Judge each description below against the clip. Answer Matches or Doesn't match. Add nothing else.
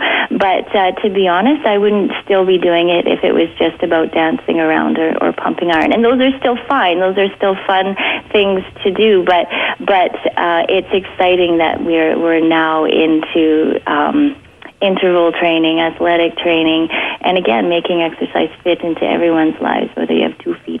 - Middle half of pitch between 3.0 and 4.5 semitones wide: Matches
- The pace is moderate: Matches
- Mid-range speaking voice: Matches